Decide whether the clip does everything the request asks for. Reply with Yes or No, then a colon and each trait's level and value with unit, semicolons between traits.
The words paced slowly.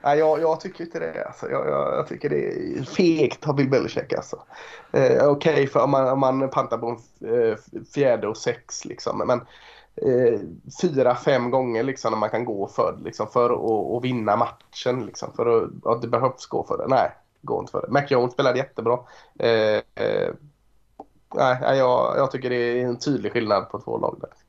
No: average, 185 wpm